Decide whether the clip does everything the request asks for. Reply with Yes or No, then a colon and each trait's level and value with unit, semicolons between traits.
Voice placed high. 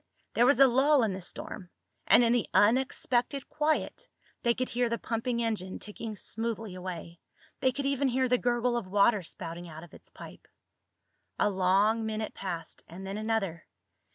Yes: high, 225 Hz